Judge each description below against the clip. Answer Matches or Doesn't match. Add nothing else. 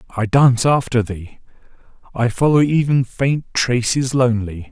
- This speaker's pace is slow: Matches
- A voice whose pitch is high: Doesn't match